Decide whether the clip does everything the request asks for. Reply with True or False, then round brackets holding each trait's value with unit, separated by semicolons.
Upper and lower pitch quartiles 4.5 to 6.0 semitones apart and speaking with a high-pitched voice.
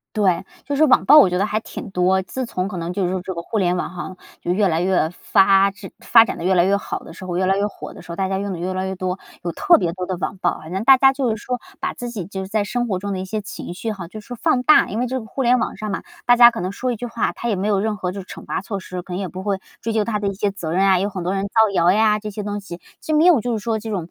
False (3.1 semitones; 200 Hz)